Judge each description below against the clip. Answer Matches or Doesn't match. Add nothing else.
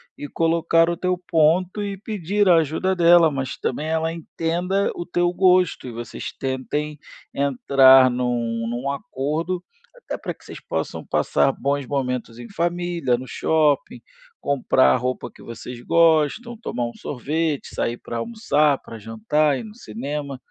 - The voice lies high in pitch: Doesn't match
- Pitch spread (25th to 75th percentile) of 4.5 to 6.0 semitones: Matches